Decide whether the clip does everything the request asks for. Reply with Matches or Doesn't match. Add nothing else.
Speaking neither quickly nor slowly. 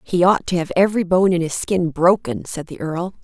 Doesn't match